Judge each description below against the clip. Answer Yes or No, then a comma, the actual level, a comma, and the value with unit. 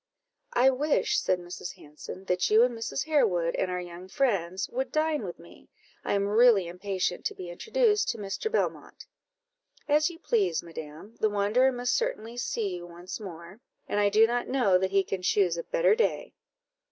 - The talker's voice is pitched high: Yes, high, 205 Hz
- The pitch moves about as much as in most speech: No, wide, 5.7 semitones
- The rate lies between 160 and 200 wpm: Yes, average, 185 wpm